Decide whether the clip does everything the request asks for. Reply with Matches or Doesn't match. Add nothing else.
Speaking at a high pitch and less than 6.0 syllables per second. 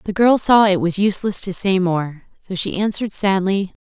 Matches